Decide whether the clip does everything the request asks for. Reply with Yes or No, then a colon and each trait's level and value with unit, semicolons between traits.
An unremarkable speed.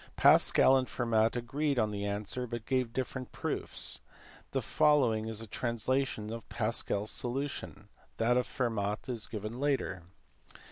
Yes: average, 145 wpm